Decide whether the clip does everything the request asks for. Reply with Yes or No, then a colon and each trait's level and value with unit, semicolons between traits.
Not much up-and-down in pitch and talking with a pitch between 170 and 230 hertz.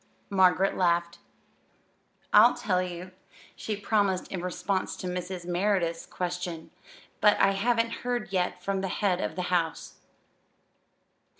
Yes: narrow, 2.1 semitones; medium, 185 Hz